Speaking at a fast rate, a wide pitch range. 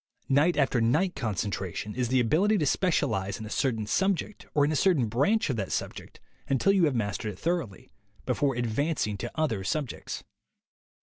No: average, 180 wpm; wide, 6.5 semitones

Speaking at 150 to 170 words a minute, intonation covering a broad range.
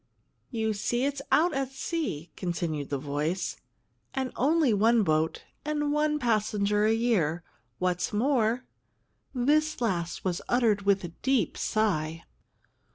No: slow, 135 wpm; wide, 7.1 semitones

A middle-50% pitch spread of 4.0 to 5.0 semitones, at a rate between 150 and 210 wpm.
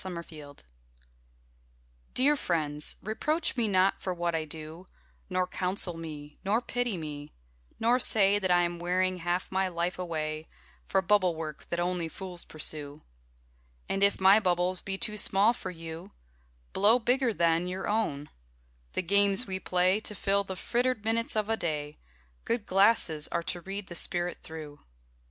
No: average, 3.6 semitones; average, 160 wpm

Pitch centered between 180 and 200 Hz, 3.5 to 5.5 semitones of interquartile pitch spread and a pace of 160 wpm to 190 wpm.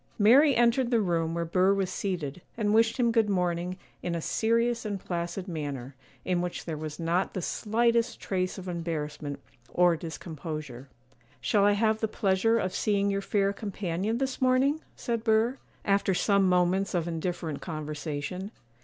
Yes: high, 190 Hz; average, 4.6 semitones; average, 165 wpm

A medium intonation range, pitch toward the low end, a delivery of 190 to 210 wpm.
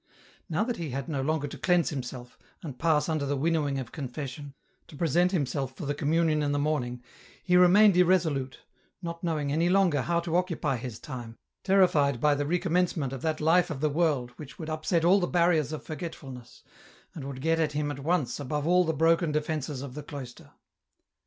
No: average, 3.3 semitones; medium, 155 Hz; average, 200 wpm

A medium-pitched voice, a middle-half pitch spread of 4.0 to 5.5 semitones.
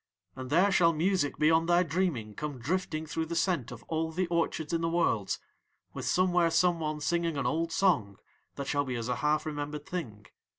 No: medium, 160 Hz; average, 3.3 semitones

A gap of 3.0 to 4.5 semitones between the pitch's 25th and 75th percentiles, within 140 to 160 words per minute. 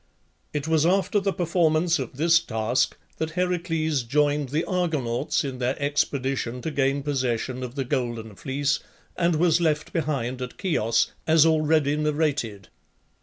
Yes: average, 4.0 semitones; average, 145 wpm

